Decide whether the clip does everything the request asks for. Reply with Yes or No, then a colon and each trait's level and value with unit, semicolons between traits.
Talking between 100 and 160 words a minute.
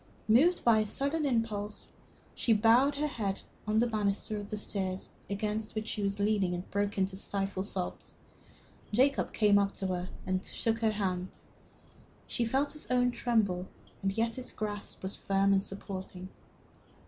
No: average, 170 wpm